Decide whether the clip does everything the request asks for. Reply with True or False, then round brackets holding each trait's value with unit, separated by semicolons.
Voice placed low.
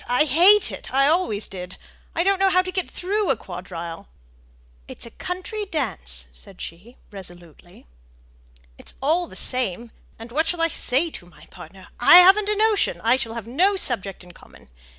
False (260 Hz)